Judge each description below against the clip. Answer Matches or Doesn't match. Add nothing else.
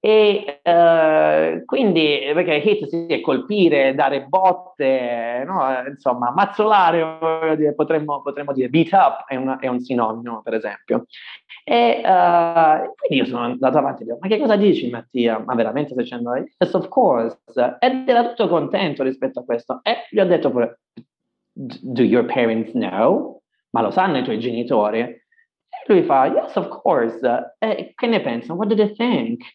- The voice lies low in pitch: Doesn't match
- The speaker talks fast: Matches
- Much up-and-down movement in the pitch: Matches